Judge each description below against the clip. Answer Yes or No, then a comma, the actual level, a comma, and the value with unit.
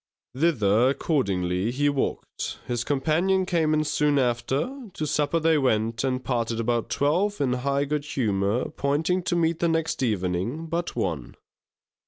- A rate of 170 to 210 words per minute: No, average, 150 wpm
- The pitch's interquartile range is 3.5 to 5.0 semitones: No, wide, 5.6 semitones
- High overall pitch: No, medium, 140 Hz